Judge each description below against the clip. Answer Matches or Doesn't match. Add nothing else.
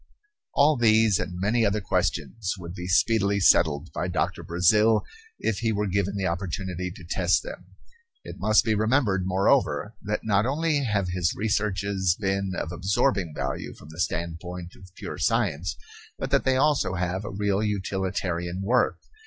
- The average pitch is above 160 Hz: Doesn't match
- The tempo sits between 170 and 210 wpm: Doesn't match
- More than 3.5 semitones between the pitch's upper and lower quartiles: Doesn't match